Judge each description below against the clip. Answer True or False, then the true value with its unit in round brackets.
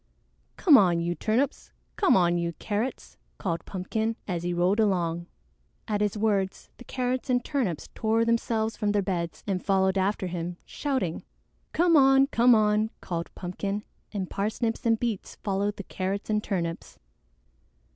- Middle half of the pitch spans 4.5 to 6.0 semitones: False (4.0 semitones)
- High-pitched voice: True (205 Hz)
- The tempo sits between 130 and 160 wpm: True (155 wpm)